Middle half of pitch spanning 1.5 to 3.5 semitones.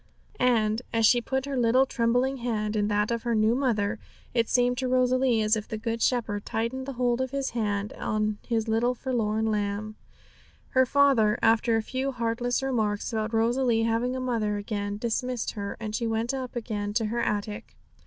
Yes: average, 2.7 semitones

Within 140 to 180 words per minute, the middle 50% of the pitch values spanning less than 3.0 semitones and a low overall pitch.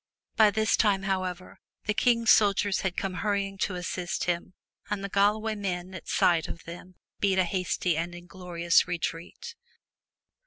No: average, 160 wpm; narrow, 2.4 semitones; high, 190 Hz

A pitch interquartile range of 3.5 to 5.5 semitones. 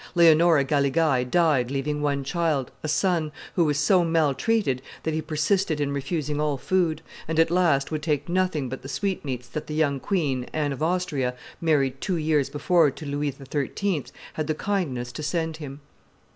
No: average, 3.1 semitones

